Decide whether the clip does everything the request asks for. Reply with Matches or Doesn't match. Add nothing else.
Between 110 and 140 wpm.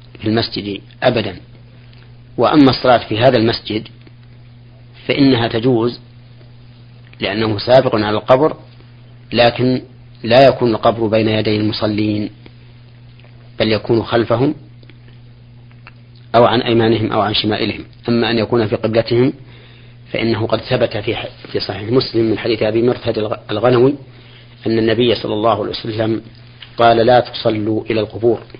Matches